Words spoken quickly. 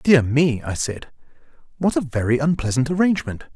No: average, 150 wpm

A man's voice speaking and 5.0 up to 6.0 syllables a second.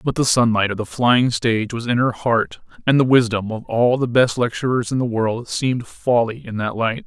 Yes: male; 5.1 syllables/s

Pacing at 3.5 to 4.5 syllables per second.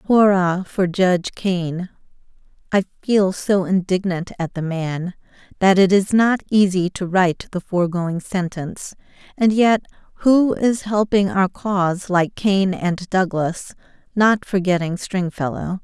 Yes: 4.1 syllables/s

